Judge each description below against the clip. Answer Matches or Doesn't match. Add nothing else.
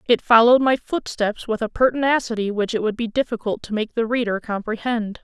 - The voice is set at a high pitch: Matches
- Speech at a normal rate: Matches